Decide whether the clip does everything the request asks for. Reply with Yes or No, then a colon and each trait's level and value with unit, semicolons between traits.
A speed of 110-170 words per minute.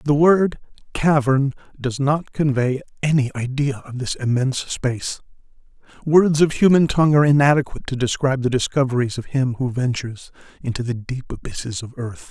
Yes: average, 155 wpm